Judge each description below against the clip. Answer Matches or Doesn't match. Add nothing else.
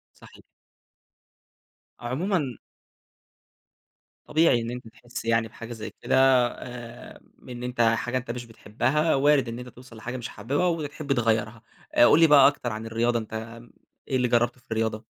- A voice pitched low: Matches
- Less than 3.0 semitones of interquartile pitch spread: Matches